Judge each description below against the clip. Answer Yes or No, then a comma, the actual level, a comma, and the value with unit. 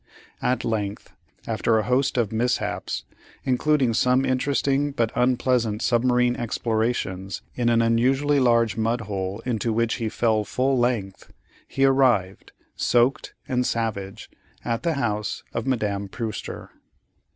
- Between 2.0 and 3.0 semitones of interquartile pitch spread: Yes, narrow, 2.6 semitones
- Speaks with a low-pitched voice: Yes, low, 120 Hz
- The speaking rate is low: Yes, slow, 130 wpm